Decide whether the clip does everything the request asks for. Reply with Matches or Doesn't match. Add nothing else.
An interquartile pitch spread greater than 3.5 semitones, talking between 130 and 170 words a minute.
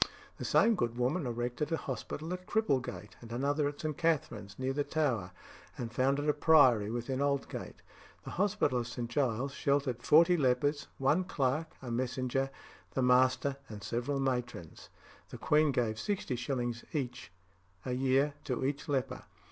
Doesn't match